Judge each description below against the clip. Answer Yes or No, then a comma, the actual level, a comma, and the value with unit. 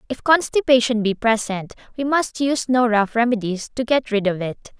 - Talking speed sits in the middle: Yes, average, 190 wpm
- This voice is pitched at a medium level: No, high, 235 Hz